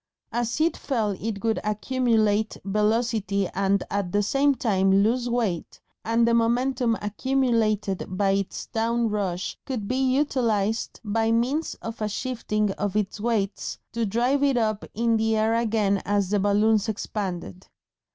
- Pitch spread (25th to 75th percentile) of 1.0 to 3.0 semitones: Yes, narrow, 2.6 semitones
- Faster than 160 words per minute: No, average, 150 wpm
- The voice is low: No, high, 220 Hz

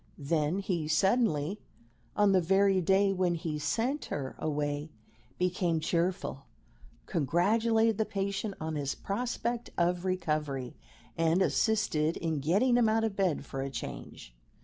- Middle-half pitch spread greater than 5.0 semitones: No, average, 4.6 semitones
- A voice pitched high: No, medium, 180 Hz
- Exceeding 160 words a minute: No, slow, 135 wpm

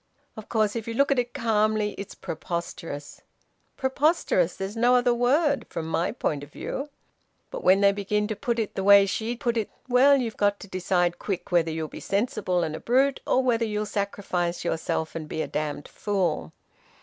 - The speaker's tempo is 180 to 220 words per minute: Yes, average, 195 wpm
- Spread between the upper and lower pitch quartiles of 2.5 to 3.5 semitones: No, average, 5.2 semitones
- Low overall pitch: No, high, 205 Hz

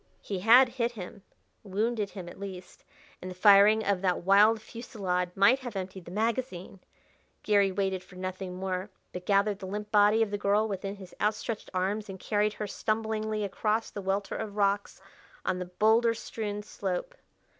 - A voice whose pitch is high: Yes, high, 205 Hz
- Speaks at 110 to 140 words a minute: No, average, 175 wpm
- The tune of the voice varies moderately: No, narrow, 2.3 semitones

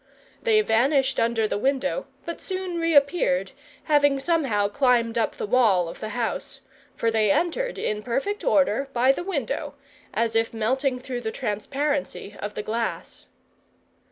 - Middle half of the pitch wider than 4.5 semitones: Yes, average, 4.9 semitones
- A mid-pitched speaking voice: No, very high, 260 Hz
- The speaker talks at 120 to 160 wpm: Yes, average, 150 wpm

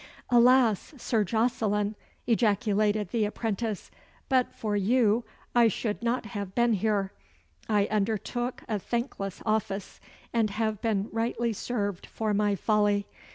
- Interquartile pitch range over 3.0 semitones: No, narrow, 2.4 semitones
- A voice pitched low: No, high, 215 Hz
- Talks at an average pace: No, slow, 125 wpm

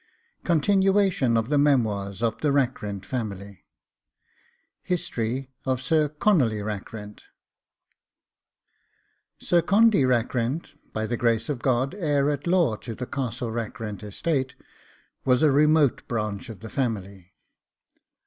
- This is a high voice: No, low, 125 Hz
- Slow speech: Yes, slow, 120 wpm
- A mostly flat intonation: No, average, 5.1 semitones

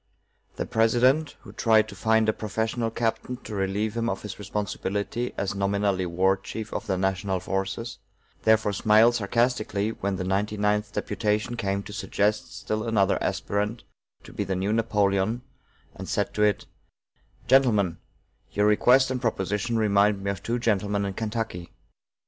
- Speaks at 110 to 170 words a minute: Yes, average, 155 wpm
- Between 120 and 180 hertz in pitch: No, low, 105 Hz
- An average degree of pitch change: No, narrow, 2.3 semitones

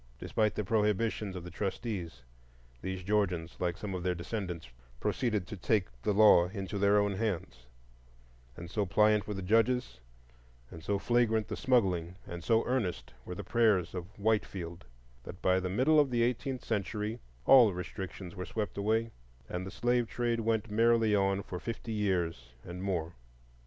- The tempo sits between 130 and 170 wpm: Yes, average, 165 wpm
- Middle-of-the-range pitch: No, low, 100 Hz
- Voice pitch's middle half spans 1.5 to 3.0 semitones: No, average, 3.8 semitones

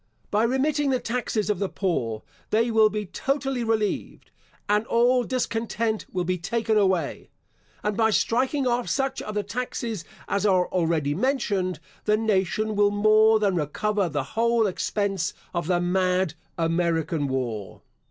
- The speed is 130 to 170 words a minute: Yes, average, 150 wpm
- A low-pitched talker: No, high, 210 Hz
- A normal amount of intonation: Yes, average, 4.3 semitones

